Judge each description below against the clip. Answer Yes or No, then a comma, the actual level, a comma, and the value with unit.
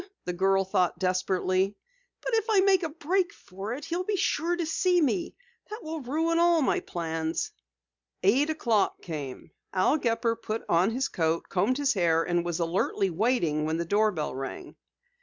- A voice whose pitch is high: Yes, high, 215 Hz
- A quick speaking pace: No, average, 175 wpm